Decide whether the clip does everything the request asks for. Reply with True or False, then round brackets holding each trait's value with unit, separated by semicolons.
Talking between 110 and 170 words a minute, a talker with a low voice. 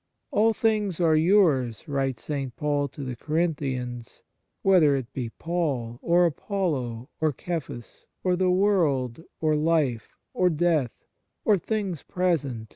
False (145 wpm; 155 Hz)